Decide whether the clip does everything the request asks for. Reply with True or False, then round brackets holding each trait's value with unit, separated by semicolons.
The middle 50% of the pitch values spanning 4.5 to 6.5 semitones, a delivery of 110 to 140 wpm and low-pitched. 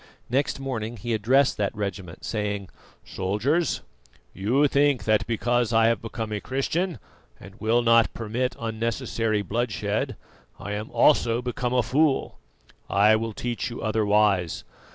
False (2.8 semitones; 135 wpm; 115 Hz)